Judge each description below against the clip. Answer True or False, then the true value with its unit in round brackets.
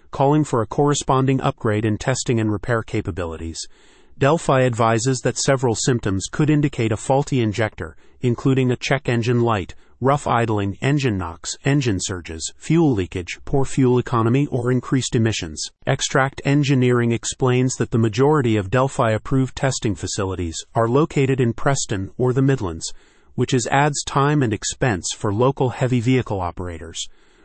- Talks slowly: False (150 wpm)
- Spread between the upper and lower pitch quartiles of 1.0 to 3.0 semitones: False (4.1 semitones)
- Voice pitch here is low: True (125 Hz)